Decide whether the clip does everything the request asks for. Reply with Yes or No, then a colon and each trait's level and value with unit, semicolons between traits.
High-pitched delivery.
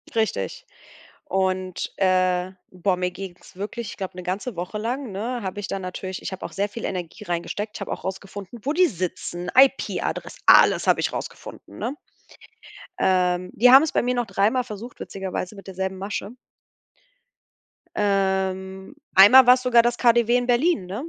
Yes: high, 195 Hz